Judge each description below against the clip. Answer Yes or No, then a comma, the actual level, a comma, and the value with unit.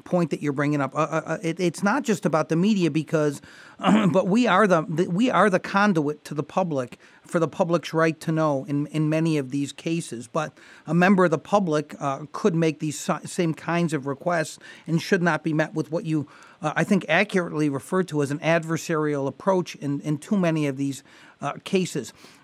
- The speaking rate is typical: No, fast, 215 wpm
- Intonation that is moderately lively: Yes, average, 3.3 semitones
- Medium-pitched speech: Yes, medium, 160 Hz